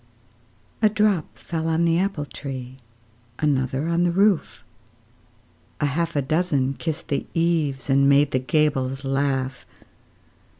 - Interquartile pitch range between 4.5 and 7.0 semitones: No, average, 3.9 semitones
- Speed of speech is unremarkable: No, slow, 130 wpm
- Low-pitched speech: No, medium, 145 Hz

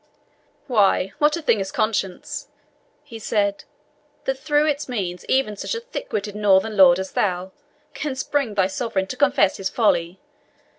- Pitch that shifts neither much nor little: No, wide, 5.8 semitones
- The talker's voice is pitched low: No, high, 210 Hz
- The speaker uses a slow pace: No, average, 160 wpm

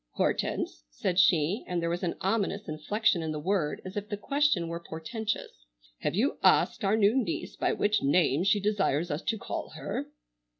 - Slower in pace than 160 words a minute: No, average, 185 wpm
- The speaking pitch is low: No, medium, 185 Hz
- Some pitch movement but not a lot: Yes, average, 4.4 semitones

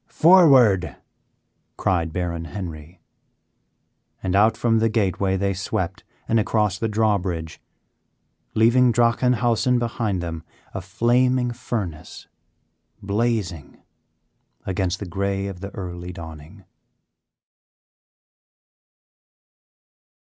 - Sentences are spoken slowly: Yes, slow, 90 wpm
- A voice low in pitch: Yes, low, 100 Hz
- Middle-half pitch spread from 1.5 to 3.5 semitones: No, average, 4.6 semitones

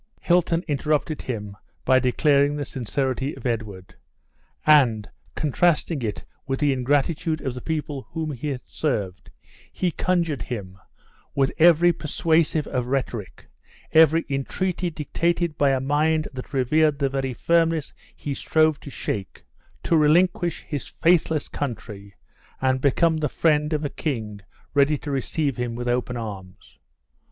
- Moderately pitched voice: Yes, medium, 145 Hz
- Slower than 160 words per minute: Yes, average, 140 wpm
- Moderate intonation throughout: Yes, average, 3.9 semitones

